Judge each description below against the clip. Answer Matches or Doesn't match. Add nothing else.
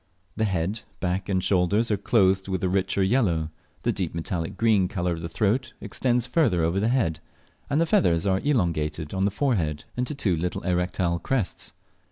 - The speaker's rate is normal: Matches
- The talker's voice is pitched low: Matches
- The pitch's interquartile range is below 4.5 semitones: Doesn't match